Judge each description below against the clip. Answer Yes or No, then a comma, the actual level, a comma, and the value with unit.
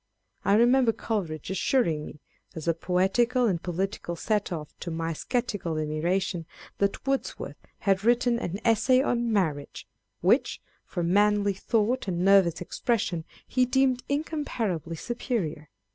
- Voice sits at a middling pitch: No, high, 200 Hz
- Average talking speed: No, slow, 130 wpm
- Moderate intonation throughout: No, wide, 5.9 semitones